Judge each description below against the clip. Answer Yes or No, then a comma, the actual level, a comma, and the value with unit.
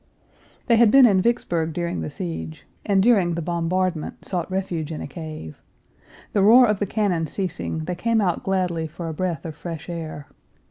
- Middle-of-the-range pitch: Yes, medium, 175 Hz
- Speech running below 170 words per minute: No, average, 185 wpm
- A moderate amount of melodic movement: Yes, average, 3.5 semitones